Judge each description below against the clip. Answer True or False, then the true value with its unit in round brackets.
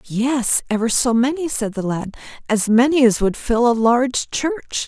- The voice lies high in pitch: True (245 Hz)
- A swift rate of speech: False (185 wpm)